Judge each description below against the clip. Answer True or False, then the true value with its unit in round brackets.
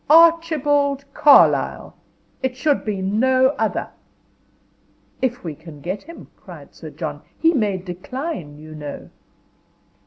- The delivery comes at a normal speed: False (120 wpm)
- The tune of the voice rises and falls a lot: True (8.3 semitones)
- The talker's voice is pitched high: True (255 Hz)